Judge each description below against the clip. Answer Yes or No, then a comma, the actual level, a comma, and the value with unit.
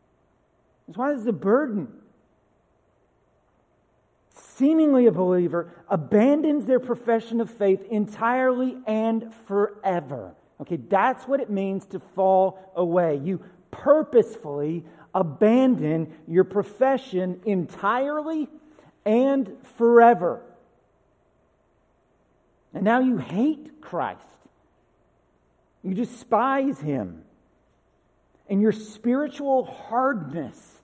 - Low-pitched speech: No, high, 215 Hz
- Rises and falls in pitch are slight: No, wide, 5.4 semitones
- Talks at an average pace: No, slow, 85 wpm